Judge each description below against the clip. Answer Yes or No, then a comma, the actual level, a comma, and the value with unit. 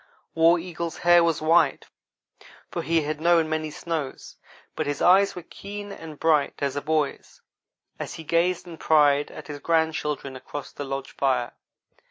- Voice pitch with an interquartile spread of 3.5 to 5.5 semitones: No, narrow, 2.6 semitones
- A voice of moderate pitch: Yes, medium, 160 Hz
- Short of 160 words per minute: No, average, 165 wpm